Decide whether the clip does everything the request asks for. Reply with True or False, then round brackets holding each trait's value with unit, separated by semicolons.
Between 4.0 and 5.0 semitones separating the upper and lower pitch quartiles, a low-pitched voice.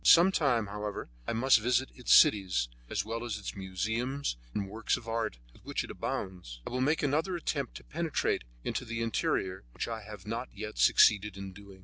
True (4.3 semitones; 110 Hz)